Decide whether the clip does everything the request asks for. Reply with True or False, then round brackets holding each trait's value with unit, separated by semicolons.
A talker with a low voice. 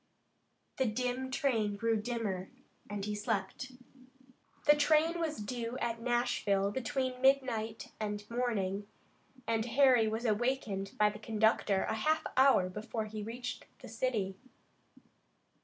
False (230 Hz)